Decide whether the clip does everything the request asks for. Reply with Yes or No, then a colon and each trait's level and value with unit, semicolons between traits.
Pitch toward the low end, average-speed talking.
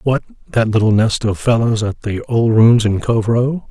No: low, 110 Hz; fast, 210 wpm